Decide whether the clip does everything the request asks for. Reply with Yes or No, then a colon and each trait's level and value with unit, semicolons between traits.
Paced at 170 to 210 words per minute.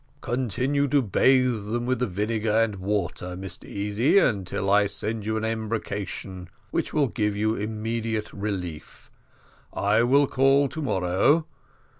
No: slow, 135 wpm